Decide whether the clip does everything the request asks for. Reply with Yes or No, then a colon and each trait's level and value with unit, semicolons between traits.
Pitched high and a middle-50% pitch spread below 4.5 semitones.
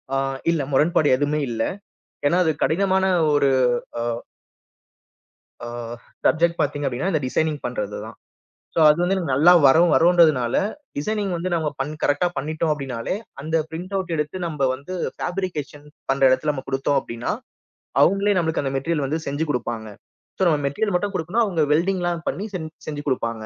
No: medium, 155 Hz; average, 4.1 semitones